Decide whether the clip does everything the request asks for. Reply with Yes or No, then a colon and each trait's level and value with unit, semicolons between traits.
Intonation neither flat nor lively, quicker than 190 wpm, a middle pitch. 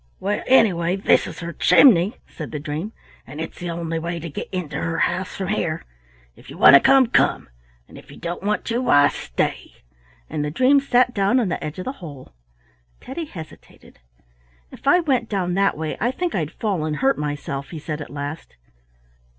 No: wide, 6.6 semitones; average, 200 wpm; medium, 175 Hz